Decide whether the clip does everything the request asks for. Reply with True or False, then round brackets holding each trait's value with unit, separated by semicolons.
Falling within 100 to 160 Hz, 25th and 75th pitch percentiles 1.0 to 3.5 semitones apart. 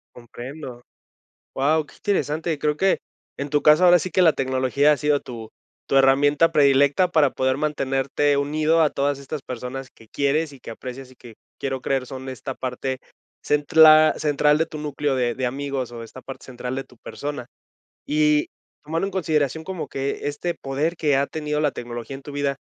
True (140 Hz; 2.5 semitones)